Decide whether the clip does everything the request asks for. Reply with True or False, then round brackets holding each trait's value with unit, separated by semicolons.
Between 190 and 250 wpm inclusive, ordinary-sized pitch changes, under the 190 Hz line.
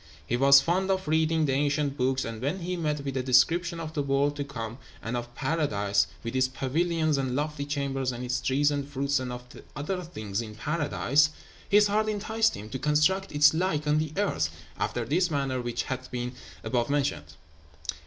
True (200 wpm; 3.9 semitones; 140 Hz)